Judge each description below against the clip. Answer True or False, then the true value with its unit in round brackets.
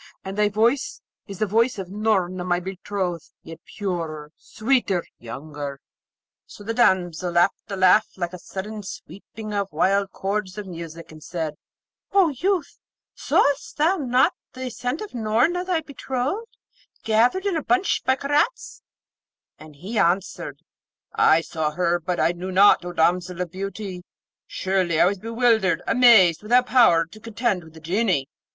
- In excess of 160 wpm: False (155 wpm)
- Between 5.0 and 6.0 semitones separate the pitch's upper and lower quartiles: True (5.3 semitones)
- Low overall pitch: False (195 Hz)